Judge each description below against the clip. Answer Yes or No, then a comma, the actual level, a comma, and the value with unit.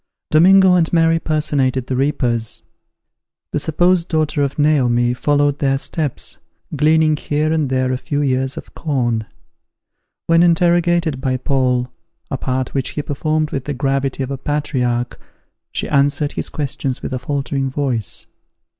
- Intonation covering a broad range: No, average, 3.0 semitones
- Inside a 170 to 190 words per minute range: No, average, 145 wpm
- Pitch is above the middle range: No, medium, 140 Hz